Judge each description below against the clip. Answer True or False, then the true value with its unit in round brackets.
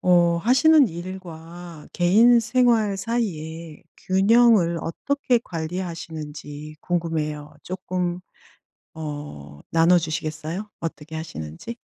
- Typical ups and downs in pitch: True (3.9 semitones)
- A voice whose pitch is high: False (170 Hz)